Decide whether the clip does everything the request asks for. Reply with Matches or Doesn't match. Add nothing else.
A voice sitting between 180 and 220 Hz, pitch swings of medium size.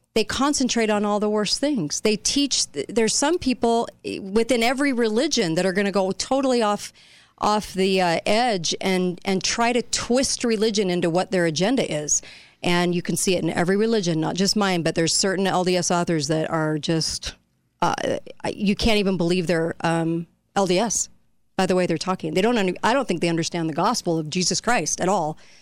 Matches